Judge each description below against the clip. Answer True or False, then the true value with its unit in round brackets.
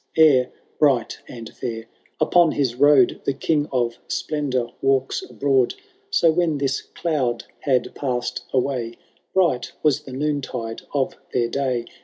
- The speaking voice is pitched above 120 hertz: True (135 Hz)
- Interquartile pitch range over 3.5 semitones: False (3.1 semitones)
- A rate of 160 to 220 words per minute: False (135 wpm)